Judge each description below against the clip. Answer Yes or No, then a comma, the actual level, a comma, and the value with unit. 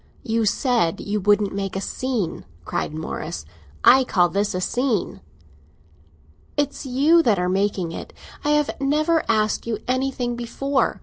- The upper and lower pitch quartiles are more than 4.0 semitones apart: Yes, wide, 5.4 semitones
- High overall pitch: Yes, high, 230 Hz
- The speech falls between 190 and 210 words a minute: No, average, 145 wpm